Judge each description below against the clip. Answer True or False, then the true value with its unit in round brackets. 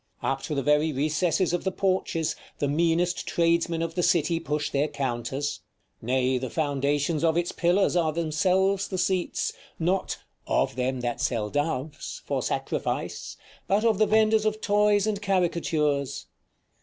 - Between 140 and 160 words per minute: True (155 wpm)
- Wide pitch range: False (4.5 semitones)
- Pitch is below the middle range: False (165 Hz)